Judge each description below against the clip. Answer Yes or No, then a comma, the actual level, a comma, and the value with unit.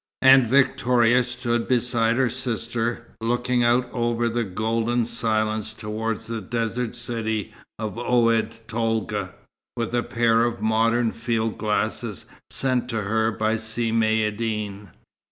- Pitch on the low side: Yes, low, 115 Hz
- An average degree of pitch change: No, narrow, 1.5 semitones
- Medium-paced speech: No, slow, 125 wpm